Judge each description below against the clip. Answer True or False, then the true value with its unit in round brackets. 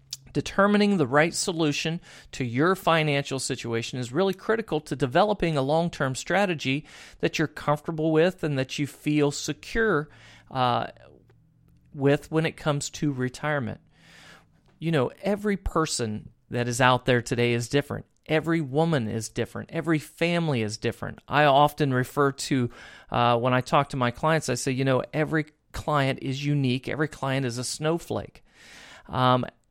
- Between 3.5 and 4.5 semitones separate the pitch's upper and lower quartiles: True (4.1 semitones)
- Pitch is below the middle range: False (145 Hz)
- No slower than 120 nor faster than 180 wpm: True (155 wpm)